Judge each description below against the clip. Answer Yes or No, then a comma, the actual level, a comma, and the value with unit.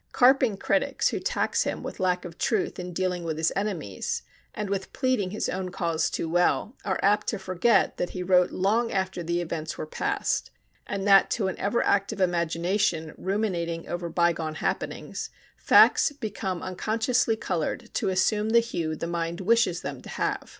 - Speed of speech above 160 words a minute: Yes, average, 175 wpm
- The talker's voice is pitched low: No, medium, 185 Hz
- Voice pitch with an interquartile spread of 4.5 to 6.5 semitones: No, average, 3.4 semitones